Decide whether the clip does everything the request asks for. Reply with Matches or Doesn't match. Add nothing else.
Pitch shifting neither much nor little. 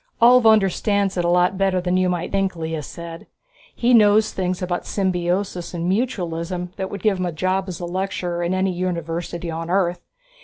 Doesn't match